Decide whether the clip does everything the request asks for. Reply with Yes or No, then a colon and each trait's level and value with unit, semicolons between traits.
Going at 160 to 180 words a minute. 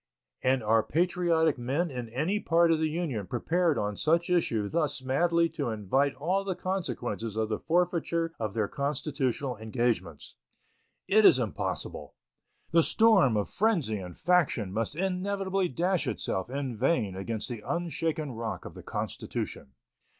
No: average, 150 wpm